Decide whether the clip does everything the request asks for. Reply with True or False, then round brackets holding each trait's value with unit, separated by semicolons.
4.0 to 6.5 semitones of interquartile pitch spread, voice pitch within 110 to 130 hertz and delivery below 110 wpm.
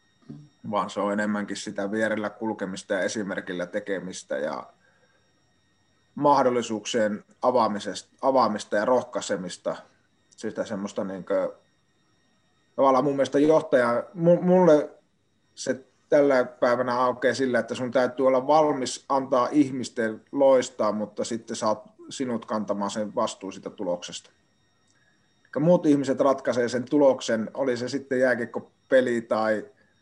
False (4.3 semitones; 125 Hz; 120 wpm)